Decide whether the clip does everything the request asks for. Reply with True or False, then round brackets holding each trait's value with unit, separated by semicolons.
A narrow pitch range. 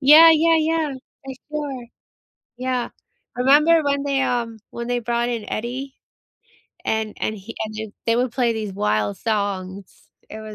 False (4.3 semitones)